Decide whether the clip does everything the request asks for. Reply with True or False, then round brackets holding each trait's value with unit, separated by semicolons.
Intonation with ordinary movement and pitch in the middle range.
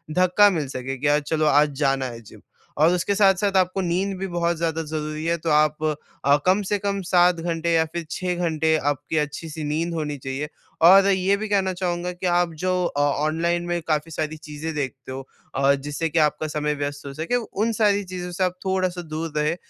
True (3.5 semitones; 165 Hz)